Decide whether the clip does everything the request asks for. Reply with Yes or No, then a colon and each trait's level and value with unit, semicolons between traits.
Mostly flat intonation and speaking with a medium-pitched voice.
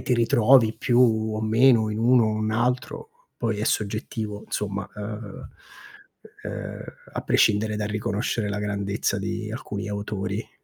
No: narrow, 1.9 semitones; low, 110 Hz